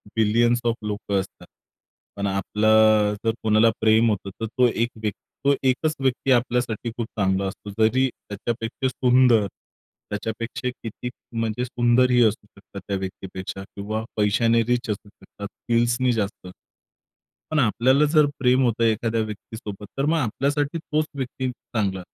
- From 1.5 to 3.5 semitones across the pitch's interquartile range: Yes, average, 3.0 semitones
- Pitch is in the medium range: No, low, 115 Hz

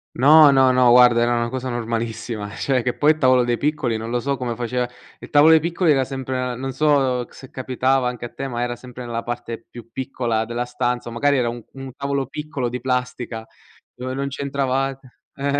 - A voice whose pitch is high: No, low, 125 Hz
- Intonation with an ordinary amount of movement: No, narrow, 2.1 semitones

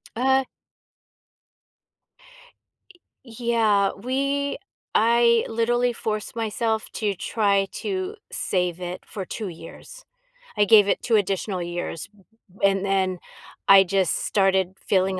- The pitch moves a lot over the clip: No, average, 3.5 semitones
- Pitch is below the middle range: No, high, 210 Hz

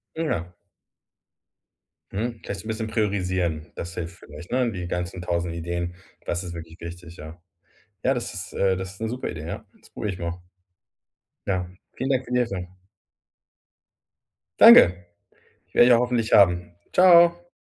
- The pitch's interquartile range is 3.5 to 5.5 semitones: Yes, average, 4.9 semitones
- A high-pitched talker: No, very low, 90 Hz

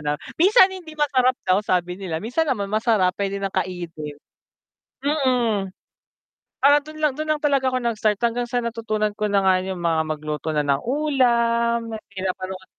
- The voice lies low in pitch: No, high, 220 Hz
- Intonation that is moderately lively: No, wide, 5.8 semitones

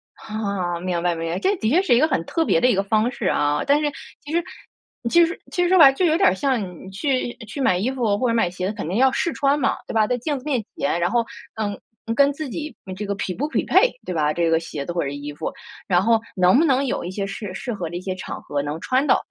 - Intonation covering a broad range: Yes, wide, 7.5 semitones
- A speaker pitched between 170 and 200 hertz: No, high, 220 Hz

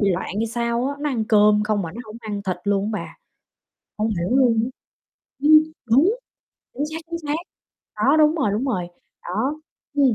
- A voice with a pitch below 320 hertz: Yes, high, 230 Hz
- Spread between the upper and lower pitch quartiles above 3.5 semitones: Yes, average, 5.0 semitones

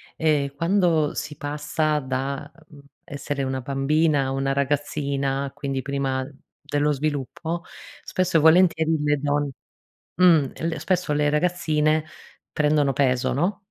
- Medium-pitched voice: Yes, medium, 145 Hz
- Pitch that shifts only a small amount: Yes, narrow, 2.3 semitones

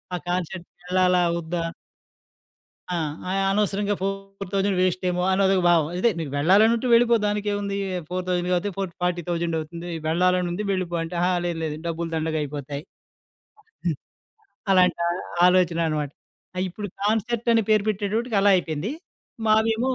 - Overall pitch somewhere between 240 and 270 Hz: No, medium, 185 Hz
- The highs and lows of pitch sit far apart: No, average, 3.0 semitones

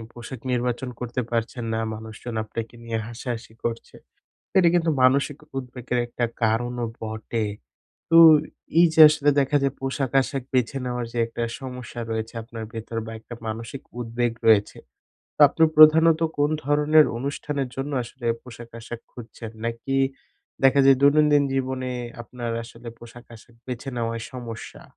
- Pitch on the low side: Yes, low, 125 Hz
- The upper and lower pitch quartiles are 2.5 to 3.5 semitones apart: Yes, average, 2.8 semitones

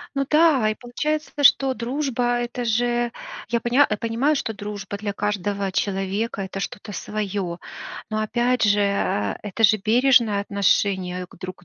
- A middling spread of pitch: Yes, average, 3.4 semitones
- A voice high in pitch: Yes, high, 215 Hz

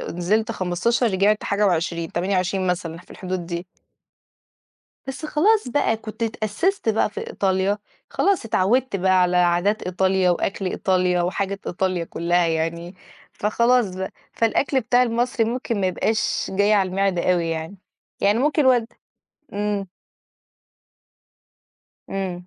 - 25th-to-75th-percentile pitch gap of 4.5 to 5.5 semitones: No, average, 3.9 semitones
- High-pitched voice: Yes, high, 195 Hz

